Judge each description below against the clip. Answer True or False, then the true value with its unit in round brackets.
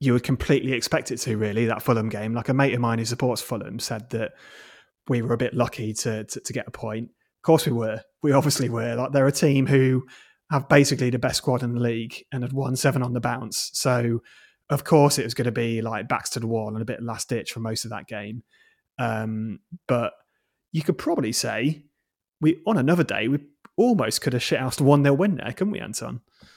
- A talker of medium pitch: False (125 Hz)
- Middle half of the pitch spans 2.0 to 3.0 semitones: False (3.5 semitones)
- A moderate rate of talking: False (235 wpm)